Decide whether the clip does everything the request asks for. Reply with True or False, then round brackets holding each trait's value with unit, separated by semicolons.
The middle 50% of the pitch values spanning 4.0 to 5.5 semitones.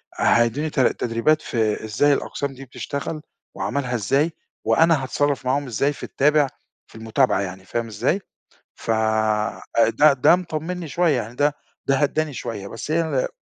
True (4.7 semitones)